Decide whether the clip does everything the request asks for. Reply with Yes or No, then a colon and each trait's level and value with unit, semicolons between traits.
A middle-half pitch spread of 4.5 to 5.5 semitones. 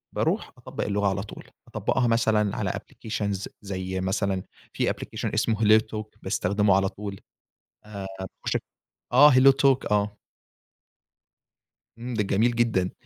No: average, 2.7 semitones